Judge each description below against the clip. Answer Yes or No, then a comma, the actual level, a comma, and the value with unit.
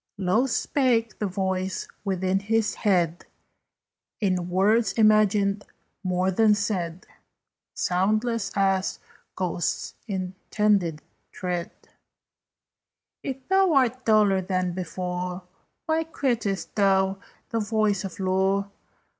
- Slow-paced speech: Yes, slow, 95 wpm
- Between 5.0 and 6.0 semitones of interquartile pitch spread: No, average, 2.8 semitones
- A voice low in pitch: No, high, 195 Hz